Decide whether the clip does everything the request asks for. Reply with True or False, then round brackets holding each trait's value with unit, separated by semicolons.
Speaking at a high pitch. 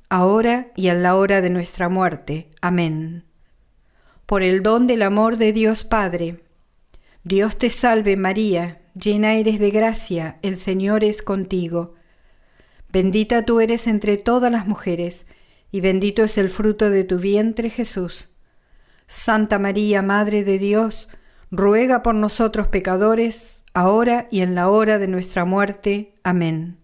True (200 Hz)